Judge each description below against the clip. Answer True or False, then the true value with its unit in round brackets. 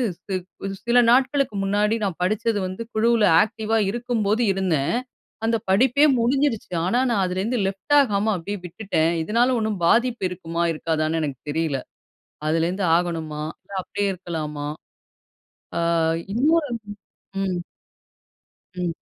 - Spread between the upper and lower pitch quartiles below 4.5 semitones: False (5.3 semitones)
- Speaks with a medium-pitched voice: False (200 Hz)